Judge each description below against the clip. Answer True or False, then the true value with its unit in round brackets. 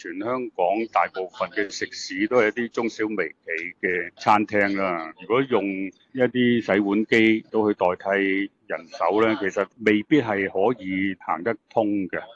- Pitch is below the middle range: True (105 Hz)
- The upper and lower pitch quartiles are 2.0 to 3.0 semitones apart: True (2.7 semitones)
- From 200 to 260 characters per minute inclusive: True (230 characters per minute)